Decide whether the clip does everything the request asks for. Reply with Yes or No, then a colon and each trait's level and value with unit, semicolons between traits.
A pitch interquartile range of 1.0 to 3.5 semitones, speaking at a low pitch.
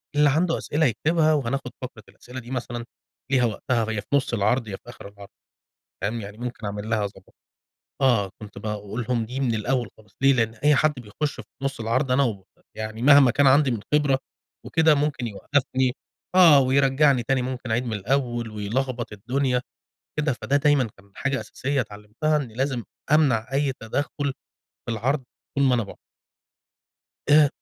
No: average, 3.9 semitones; low, 125 Hz